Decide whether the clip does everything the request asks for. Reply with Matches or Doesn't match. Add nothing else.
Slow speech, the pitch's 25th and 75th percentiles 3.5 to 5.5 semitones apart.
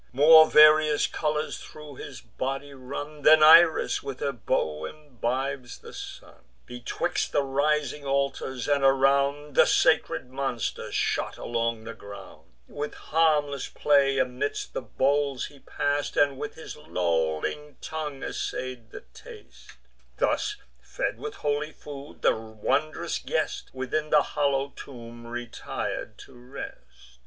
Doesn't match